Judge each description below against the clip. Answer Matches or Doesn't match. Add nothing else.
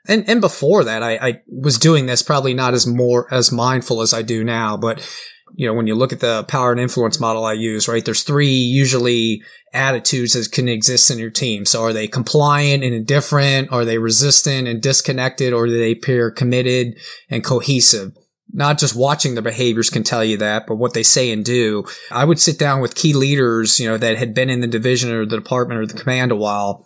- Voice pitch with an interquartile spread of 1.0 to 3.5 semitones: Matches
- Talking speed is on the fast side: Matches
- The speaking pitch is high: Doesn't match